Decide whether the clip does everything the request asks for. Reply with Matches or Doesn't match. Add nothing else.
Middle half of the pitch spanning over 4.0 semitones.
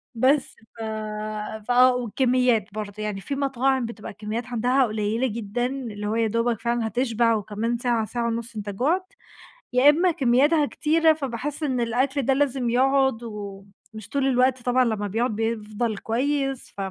Doesn't match